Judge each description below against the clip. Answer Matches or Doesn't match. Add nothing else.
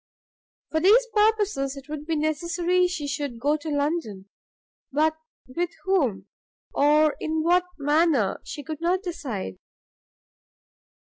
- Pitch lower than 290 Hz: Doesn't match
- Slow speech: Matches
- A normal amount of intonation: Matches